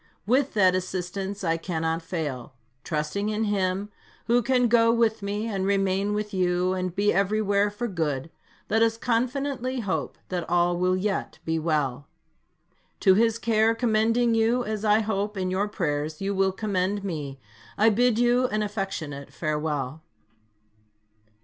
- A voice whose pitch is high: Yes, high, 200 Hz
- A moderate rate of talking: Yes, average, 150 wpm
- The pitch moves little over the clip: No, average, 4.0 semitones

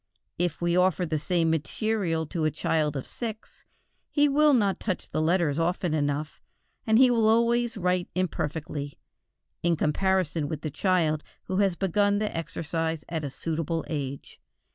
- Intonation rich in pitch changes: No, average, 4.2 semitones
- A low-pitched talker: No, medium, 170 Hz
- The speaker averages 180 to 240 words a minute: No, average, 160 wpm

